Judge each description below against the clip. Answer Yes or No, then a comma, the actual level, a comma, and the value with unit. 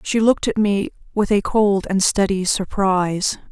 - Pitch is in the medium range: No, high, 200 Hz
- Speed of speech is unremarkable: Yes, average, 170 wpm